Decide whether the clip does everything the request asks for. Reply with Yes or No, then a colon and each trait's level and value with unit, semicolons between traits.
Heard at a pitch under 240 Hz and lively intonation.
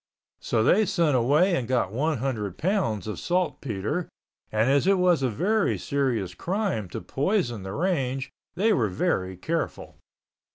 Yes: low, 135 Hz; wide, 8.4 semitones